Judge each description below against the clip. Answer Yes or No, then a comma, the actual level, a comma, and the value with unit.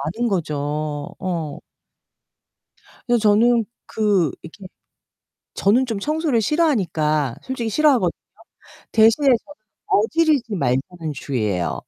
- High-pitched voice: Yes, high, 210 Hz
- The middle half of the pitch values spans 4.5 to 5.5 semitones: No, wide, 7.3 semitones